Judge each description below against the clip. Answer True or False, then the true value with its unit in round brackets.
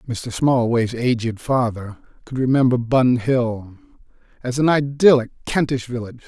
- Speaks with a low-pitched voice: True (125 Hz)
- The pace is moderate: False (125 wpm)